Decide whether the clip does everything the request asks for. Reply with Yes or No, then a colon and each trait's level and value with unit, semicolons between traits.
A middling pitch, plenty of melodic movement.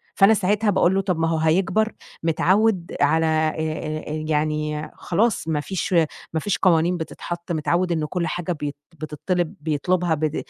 No: medium, 165 Hz; average, 2.9 semitones